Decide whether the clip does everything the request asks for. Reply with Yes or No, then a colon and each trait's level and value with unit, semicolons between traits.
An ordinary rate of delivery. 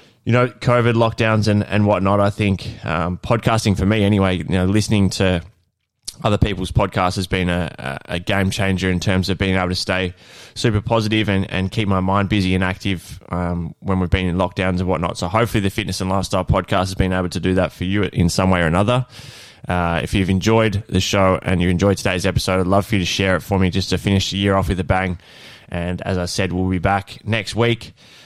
No: fast, 235 wpm